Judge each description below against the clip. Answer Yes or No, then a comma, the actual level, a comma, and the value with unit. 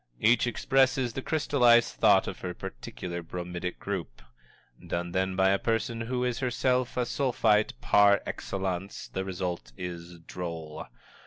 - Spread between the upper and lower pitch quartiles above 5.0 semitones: Yes, wide, 5.6 semitones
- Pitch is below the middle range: Yes, low, 100 Hz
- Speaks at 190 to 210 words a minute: No, average, 140 wpm